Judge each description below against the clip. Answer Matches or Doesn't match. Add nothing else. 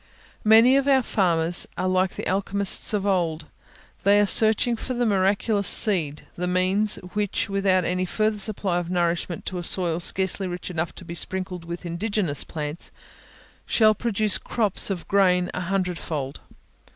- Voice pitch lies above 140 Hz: Matches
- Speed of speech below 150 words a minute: Doesn't match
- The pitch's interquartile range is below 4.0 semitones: Matches